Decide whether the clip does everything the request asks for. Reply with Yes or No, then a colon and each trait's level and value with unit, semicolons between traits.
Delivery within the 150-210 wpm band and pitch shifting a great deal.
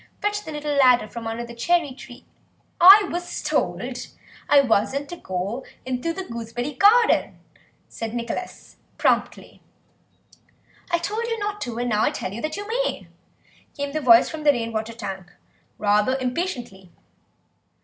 Yes: average, 155 wpm; wide, 7.0 semitones